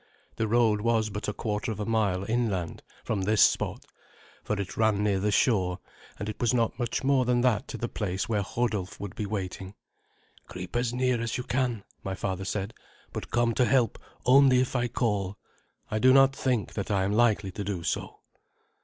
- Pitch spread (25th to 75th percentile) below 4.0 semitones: Yes, average, 3.3 semitones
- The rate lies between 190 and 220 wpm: Yes, average, 200 wpm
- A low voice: Yes, low, 110 Hz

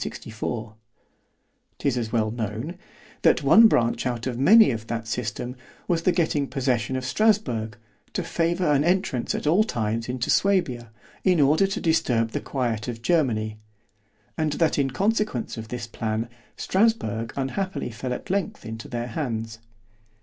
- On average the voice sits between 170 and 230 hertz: No, low, 125 Hz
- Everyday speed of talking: Yes, average, 150 wpm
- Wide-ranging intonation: Yes, wide, 6.8 semitones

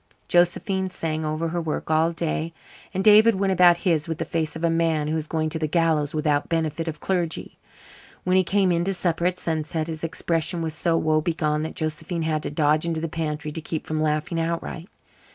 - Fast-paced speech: Yes, fast, 215 wpm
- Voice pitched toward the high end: No, medium, 165 Hz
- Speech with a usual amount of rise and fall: No, narrow, 1.7 semitones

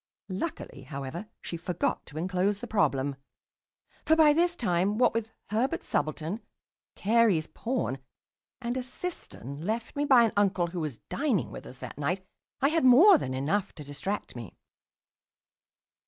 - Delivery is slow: No, average, 155 wpm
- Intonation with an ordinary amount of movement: No, wide, 8.3 semitones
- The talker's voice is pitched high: Yes, high, 195 Hz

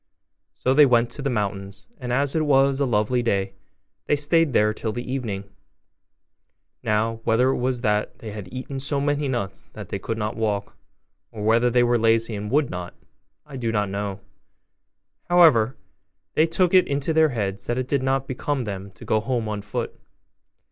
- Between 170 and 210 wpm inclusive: Yes, average, 190 wpm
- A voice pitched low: Yes, low, 120 Hz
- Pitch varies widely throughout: No, average, 4.4 semitones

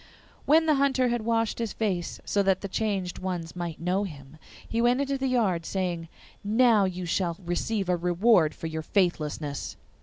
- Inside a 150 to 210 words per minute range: Yes, average, 180 wpm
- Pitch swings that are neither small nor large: Yes, average, 4.9 semitones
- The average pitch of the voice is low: No, high, 190 Hz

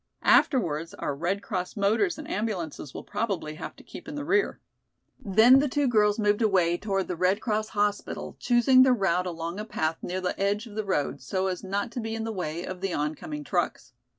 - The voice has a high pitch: Yes, high, 200 Hz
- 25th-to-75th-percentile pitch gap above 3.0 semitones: Yes, average, 4.2 semitones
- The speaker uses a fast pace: Yes, fast, 210 wpm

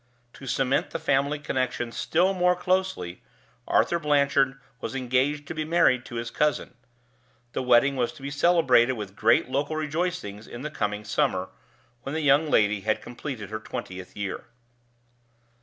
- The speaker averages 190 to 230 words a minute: No, average, 155 wpm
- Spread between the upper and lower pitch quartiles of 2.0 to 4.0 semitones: No, average, 4.5 semitones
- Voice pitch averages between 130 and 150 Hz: Yes, low, 135 Hz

